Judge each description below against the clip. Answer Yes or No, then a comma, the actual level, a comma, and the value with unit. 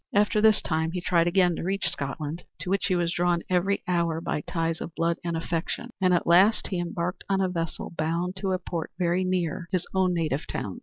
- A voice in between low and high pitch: Yes, medium, 175 Hz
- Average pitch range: No, narrow, 1.8 semitones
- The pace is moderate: No, fast, 220 wpm